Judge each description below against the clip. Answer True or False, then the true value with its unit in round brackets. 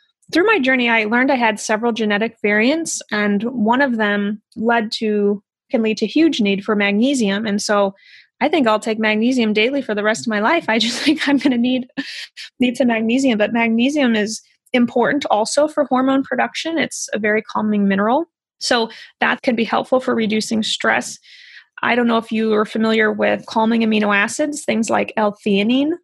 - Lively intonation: False (3.7 semitones)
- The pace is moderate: True (185 wpm)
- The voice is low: False (230 Hz)